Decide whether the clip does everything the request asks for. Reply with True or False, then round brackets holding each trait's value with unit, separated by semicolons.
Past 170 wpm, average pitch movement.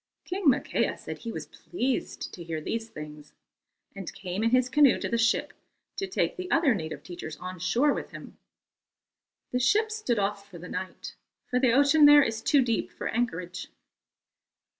False (180 wpm; 7.4 semitones)